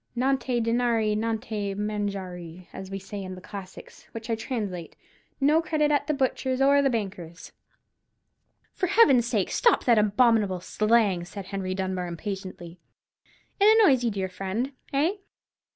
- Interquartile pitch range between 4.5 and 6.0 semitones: Yes, average, 5.2 semitones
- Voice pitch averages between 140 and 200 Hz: No, high, 215 Hz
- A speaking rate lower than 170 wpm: Yes, average, 145 wpm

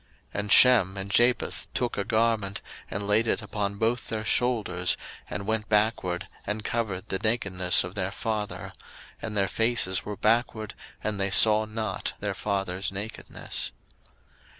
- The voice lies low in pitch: Yes, low, 105 Hz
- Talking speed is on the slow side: No, average, 150 wpm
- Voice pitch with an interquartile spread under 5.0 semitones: Yes, narrow, 2.4 semitones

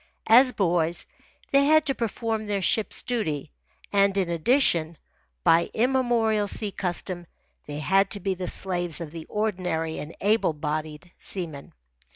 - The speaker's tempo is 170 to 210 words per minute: No, average, 155 wpm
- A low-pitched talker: No, high, 190 Hz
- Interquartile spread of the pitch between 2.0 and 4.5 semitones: No, average, 4.9 semitones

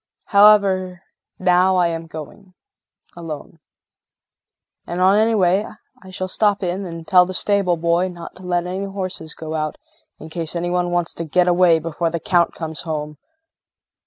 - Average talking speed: Yes, average, 165 wpm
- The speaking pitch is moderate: Yes, medium, 175 Hz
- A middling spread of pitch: No, narrow, 2.1 semitones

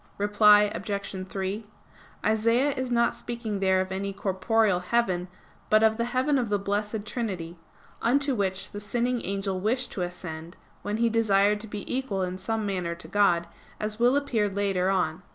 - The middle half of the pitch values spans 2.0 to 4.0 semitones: Yes, average, 3.3 semitones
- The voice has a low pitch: No, high, 205 Hz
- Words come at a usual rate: Yes, average, 175 wpm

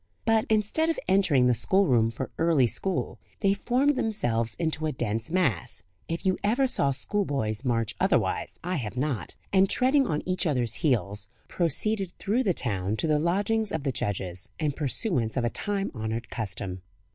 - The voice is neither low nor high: Yes, medium, 155 Hz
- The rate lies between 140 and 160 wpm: No, average, 170 wpm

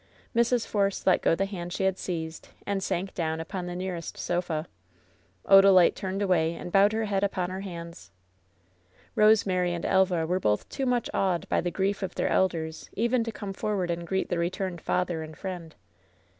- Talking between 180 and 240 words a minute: Yes, average, 190 wpm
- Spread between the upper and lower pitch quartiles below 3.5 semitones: Yes, narrow, 2.5 semitones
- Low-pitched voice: No, medium, 185 Hz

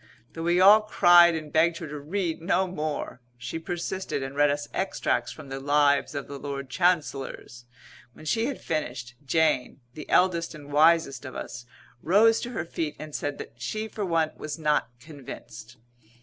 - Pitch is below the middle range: No, medium, 155 Hz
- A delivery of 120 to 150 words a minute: No, average, 175 wpm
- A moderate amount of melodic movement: Yes, average, 3.5 semitones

